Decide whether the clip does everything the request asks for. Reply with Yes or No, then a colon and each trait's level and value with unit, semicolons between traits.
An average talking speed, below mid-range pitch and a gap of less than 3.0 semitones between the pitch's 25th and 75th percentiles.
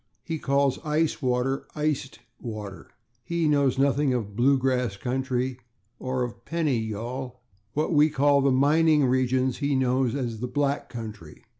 Yes: average, 145 wpm; low, 130 Hz; narrow, 2.6 semitones